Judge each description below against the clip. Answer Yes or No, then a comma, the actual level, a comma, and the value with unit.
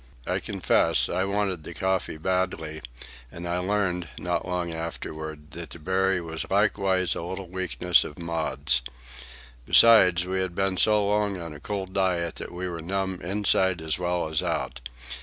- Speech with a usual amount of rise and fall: No, narrow, 2.3 semitones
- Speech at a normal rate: Yes, average, 165 wpm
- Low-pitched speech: Yes, very low, 90 Hz